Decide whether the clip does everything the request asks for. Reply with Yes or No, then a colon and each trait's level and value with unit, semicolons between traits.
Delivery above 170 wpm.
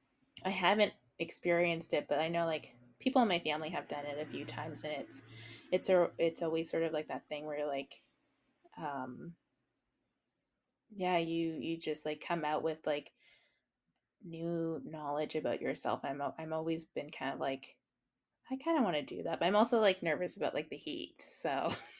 Yes: average, 190 wpm